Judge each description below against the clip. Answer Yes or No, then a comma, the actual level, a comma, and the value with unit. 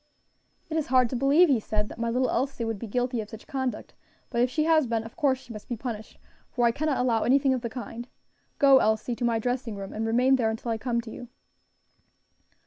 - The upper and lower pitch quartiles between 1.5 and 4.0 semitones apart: Yes, narrow, 2.6 semitones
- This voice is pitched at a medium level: No, high, 240 Hz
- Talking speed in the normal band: No, fast, 235 wpm